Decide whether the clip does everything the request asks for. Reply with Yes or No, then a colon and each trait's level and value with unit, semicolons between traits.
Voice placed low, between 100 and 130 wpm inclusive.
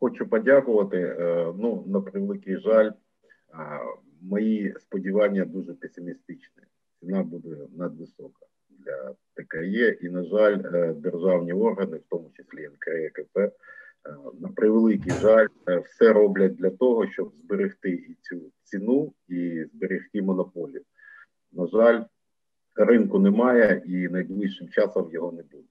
Yes: low, 105 Hz; average, 110 wpm